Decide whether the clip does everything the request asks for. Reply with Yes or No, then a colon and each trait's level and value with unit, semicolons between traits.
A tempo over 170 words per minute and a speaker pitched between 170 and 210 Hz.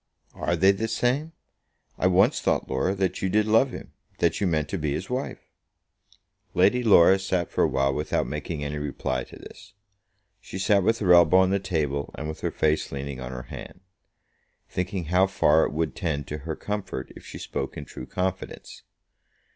No: average, 195 wpm; very low, 90 Hz